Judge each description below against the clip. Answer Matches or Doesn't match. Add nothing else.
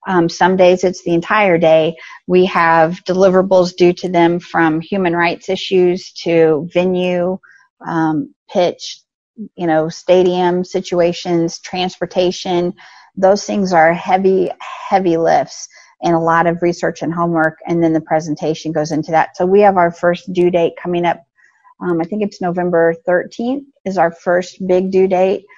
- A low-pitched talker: Doesn't match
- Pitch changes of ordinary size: Doesn't match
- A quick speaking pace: Doesn't match